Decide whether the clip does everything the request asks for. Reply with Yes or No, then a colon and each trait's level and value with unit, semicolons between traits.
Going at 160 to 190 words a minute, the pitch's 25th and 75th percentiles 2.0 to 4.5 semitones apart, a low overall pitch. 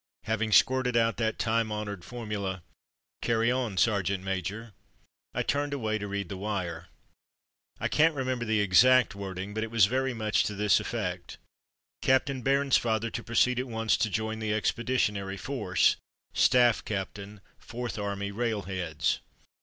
Yes: average, 170 wpm; average, 3.3 semitones; low, 110 Hz